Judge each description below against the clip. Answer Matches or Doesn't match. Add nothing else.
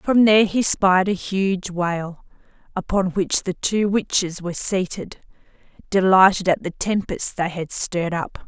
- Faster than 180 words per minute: Doesn't match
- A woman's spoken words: Matches